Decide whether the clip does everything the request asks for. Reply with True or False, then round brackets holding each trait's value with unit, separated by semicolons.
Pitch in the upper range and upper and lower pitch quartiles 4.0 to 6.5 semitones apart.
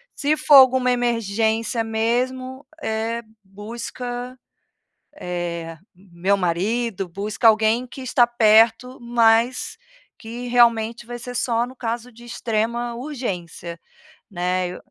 False (230 Hz; 2.7 semitones)